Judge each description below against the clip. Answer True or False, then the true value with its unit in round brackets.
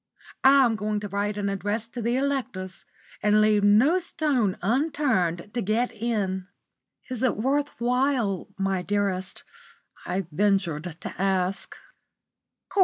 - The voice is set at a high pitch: True (210 Hz)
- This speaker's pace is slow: True (125 wpm)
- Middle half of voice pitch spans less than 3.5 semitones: False (4.3 semitones)